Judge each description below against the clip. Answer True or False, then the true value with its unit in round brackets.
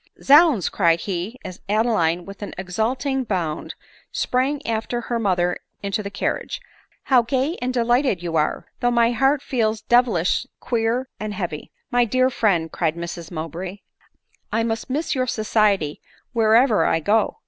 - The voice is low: False (220 Hz)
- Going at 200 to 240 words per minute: False (165 wpm)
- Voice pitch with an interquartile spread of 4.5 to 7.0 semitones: True (5.5 semitones)